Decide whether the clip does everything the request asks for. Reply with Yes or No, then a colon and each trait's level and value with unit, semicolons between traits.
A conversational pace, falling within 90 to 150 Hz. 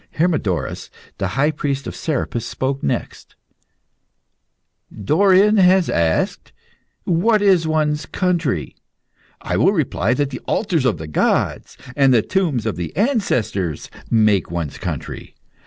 No: slow, 125 wpm; medium, 140 Hz